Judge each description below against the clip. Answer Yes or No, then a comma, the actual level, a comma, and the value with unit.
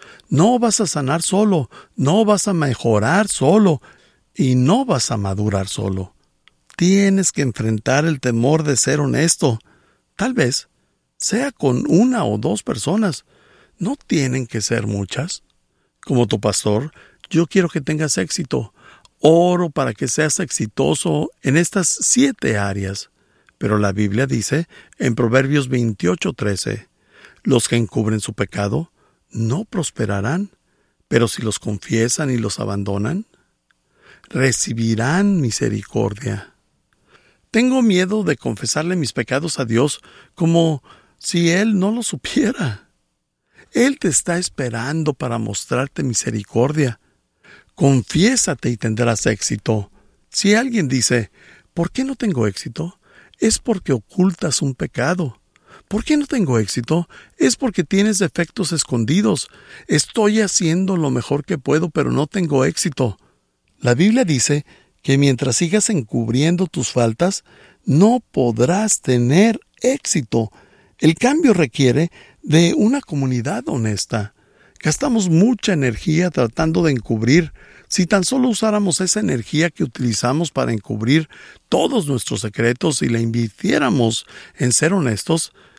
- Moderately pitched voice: Yes, medium, 145 Hz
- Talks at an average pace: No, slow, 125 wpm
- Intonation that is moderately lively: No, wide, 7.9 semitones